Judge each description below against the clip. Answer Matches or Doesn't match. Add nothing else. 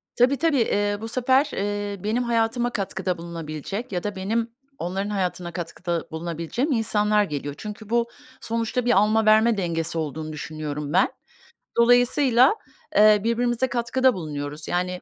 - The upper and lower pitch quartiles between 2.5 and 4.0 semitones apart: Doesn't match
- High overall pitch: Matches